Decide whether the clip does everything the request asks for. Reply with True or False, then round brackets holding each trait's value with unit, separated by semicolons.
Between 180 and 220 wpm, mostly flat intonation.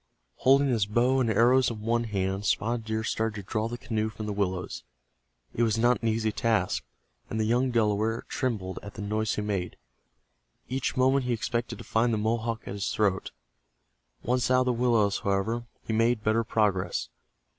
True (190 wpm; 2.2 semitones)